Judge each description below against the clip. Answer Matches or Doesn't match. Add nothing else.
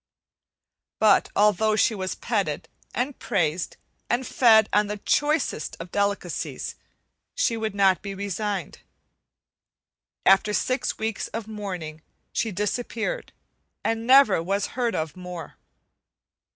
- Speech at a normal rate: Doesn't match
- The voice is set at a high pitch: Matches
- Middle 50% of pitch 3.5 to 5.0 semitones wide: Doesn't match